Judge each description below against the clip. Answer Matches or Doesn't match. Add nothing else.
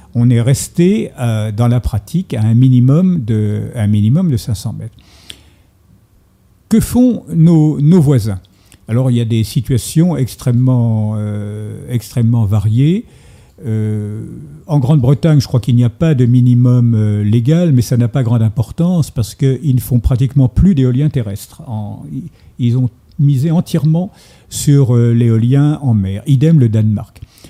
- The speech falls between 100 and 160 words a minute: Matches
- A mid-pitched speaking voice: Doesn't match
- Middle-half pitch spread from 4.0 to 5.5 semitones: Matches